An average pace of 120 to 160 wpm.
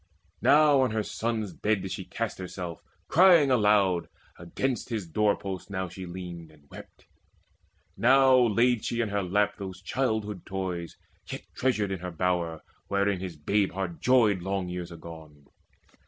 Yes: average, 155 wpm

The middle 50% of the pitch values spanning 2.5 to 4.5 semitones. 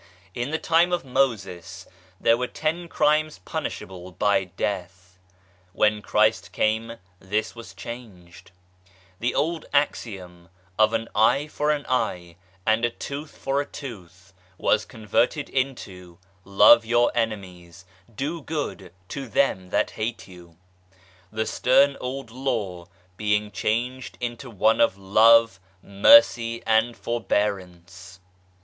No: average, 5.1 semitones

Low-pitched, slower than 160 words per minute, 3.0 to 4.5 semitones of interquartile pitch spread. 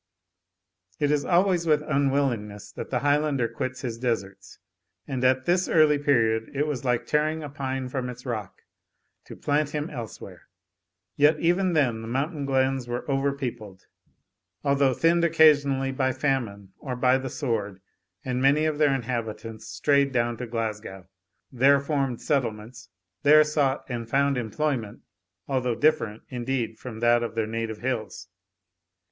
Yes: low, 130 Hz; average, 150 wpm; average, 3.7 semitones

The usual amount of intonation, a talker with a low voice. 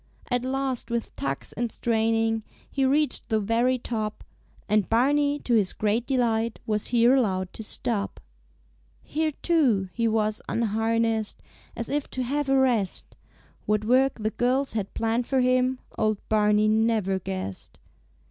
No: average, 3.0 semitones; high, 230 Hz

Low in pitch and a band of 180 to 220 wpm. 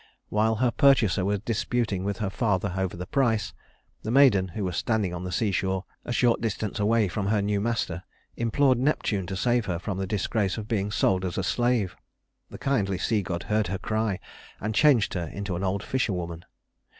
Yes: low, 105 Hz; average, 195 wpm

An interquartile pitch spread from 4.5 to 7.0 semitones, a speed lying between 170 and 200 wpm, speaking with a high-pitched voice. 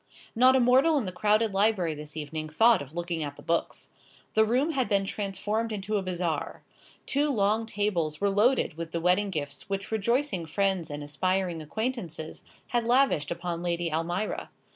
Yes: average, 5.1 semitones; average, 175 wpm; high, 195 Hz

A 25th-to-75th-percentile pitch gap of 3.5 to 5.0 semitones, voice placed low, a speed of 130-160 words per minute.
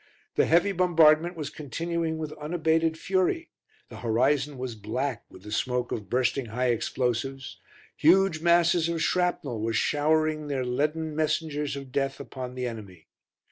No: average, 4.3 semitones; medium, 150 Hz; average, 145 wpm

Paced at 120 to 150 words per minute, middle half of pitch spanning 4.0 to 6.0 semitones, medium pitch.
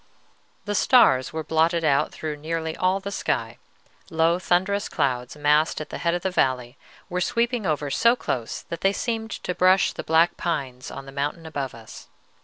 No: average, 185 wpm; average, 4.6 semitones; medium, 160 Hz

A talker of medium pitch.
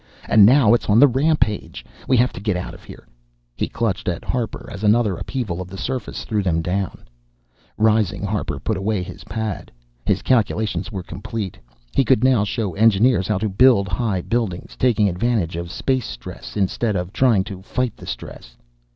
No: low, 105 Hz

